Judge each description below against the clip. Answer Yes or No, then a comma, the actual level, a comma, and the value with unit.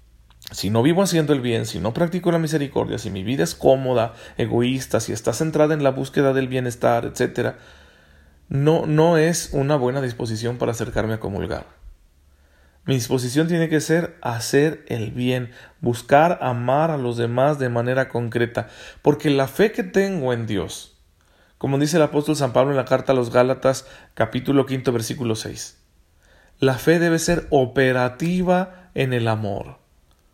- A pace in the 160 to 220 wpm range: Yes, average, 165 wpm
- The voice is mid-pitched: No, low, 125 Hz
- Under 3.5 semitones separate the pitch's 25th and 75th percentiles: No, average, 5.2 semitones